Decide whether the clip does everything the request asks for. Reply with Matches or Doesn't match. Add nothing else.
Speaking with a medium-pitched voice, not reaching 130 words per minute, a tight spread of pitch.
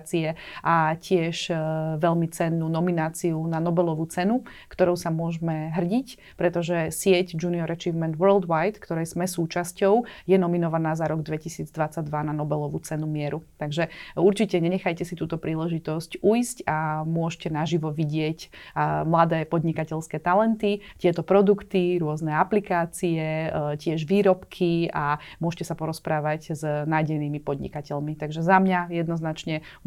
Matches